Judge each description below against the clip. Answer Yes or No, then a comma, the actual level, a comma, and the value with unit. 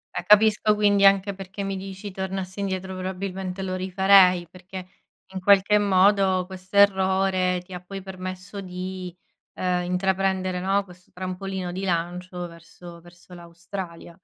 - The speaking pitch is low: No, medium, 185 Hz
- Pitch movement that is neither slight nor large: No, narrow, 1.2 semitones